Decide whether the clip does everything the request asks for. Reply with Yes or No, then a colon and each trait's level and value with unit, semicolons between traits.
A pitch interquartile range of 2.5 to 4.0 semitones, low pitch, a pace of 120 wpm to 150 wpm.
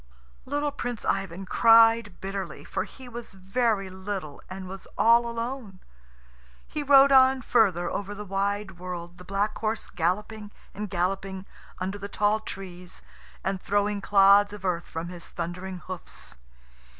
No: average, 3.3 semitones; high, 200 Hz; average, 145 wpm